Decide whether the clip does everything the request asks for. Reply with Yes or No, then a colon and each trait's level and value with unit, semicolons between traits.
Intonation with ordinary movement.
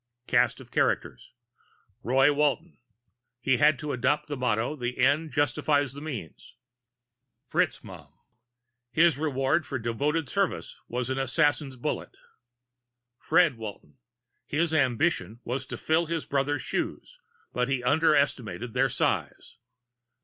Yes: average, 3.4 semitones